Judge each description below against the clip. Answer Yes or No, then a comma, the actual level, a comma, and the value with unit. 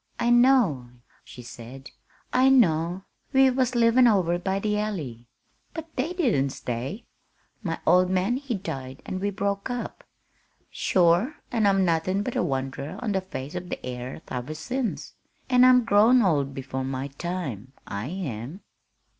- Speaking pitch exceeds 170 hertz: Yes, medium, 185 Hz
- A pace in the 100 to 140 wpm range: No, average, 155 wpm